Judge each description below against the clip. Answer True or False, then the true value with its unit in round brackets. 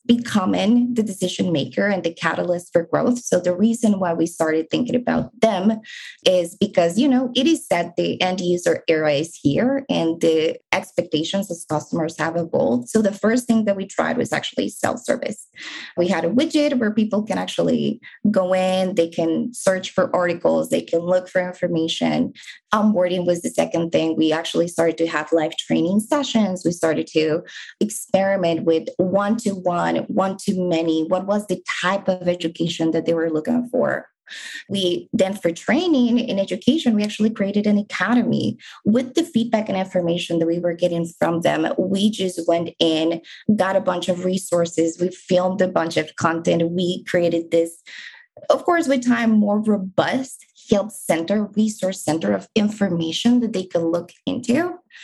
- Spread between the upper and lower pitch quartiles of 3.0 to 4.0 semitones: False (4.8 semitones)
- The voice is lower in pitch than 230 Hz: True (185 Hz)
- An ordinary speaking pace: True (170 wpm)